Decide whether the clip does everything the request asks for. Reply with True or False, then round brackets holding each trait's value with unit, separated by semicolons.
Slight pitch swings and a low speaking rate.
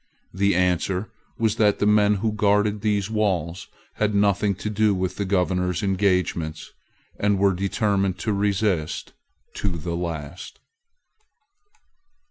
True (2.3 semitones; 125 wpm)